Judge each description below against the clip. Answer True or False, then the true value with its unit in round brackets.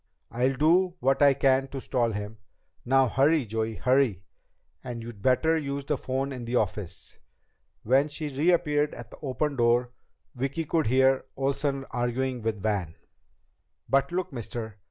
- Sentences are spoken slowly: False (155 wpm)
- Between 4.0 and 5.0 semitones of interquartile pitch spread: False (3.1 semitones)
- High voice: False (130 Hz)